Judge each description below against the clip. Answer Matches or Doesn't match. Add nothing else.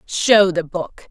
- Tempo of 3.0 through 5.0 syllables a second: Matches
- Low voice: Doesn't match